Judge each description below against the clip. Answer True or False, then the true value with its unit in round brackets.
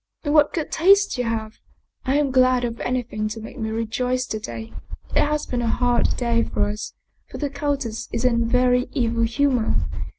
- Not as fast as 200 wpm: False (205 wpm)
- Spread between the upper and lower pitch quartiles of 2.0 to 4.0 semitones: True (3.1 semitones)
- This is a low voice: False (245 Hz)